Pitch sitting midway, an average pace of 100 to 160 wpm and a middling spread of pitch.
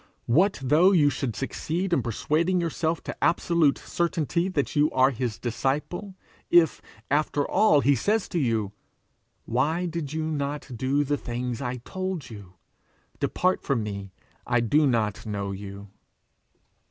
No: medium, 145 Hz; average, 145 wpm; wide, 6.1 semitones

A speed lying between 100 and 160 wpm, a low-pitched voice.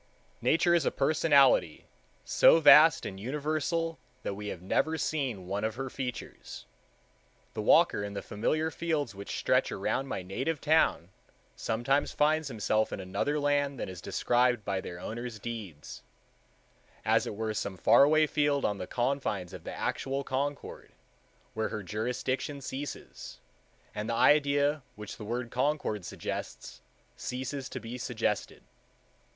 Yes: average, 145 wpm; low, 125 Hz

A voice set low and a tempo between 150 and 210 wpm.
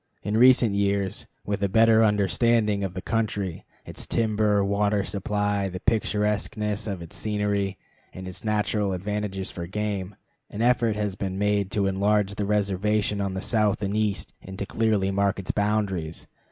Yes: low, 105 Hz; average, 165 wpm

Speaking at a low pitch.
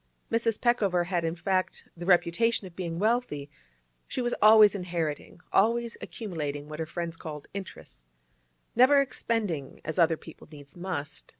No: medium, 180 Hz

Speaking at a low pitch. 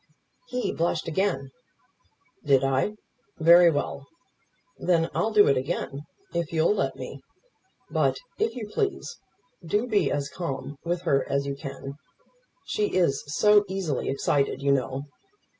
No: medium, 160 Hz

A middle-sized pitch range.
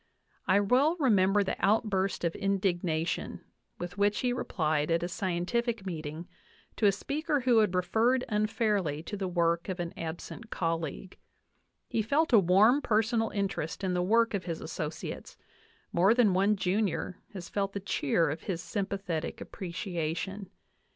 Yes: average, 3.9 semitones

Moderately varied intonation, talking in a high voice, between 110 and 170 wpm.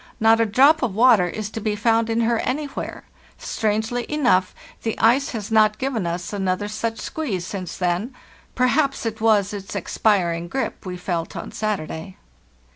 Yes: average, 3.8 semitones; high, 215 Hz; average, 165 wpm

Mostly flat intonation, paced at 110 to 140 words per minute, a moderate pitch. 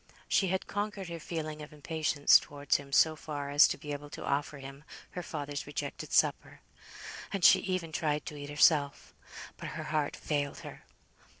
No: narrow, 2.2 semitones; average, 180 wpm; medium, 150 Hz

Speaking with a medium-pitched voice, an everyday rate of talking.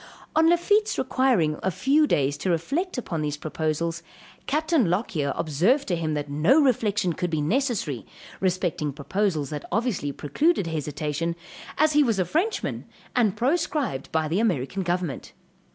Yes: medium, 180 Hz; average, 150 wpm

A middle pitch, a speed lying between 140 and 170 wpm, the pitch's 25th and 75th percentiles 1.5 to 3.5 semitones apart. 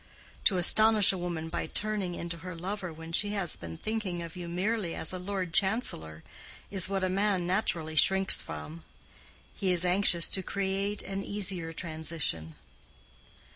Yes: medium, 180 Hz; average, 160 wpm; average, 3.0 semitones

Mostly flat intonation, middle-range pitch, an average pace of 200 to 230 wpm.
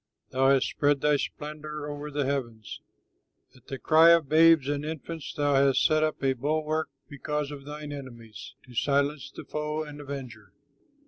No: narrow, 1.9 semitones; medium, 145 Hz; average, 170 wpm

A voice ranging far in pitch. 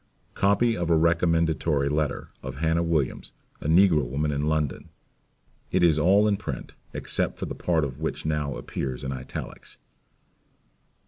No: average, 3.0 semitones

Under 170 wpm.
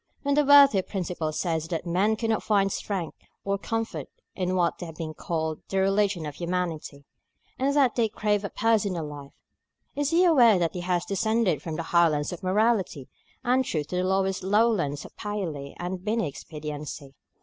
No: average, 175 wpm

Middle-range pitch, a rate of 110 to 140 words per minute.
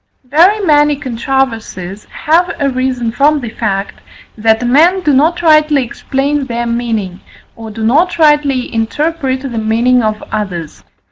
No: very high, 260 Hz; slow, 135 wpm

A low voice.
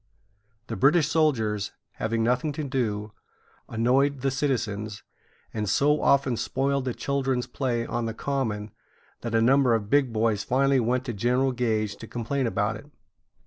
Yes: low, 125 Hz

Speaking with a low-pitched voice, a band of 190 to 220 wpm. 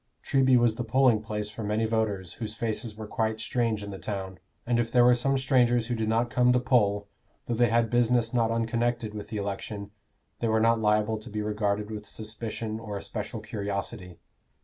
Yes: low, 110 Hz; average, 200 wpm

